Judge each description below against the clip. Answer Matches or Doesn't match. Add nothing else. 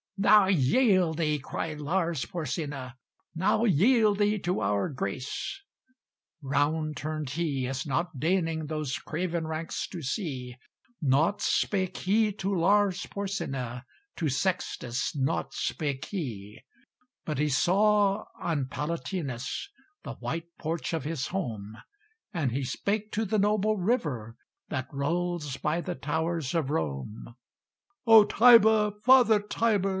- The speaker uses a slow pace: Matches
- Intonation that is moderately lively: Doesn't match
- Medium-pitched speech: Matches